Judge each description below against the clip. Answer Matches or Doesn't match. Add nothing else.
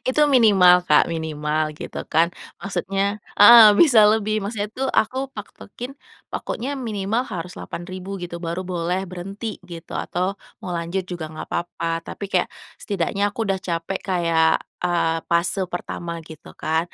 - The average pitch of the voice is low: Doesn't match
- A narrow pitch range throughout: Doesn't match